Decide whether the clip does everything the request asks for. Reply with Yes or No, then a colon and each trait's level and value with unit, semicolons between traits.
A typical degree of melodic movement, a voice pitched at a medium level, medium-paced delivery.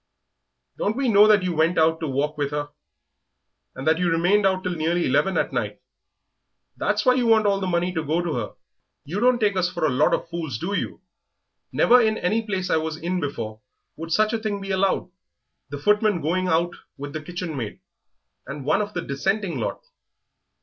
No: average, 4.5 semitones; medium, 175 Hz; fast, 210 wpm